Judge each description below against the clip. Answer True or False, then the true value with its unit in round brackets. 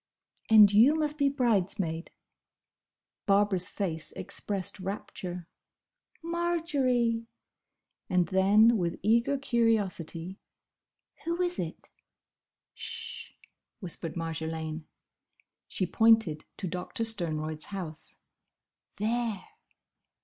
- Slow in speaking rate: True (85 wpm)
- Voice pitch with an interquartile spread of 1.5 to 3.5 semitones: False (5.4 semitones)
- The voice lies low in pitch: False (200 Hz)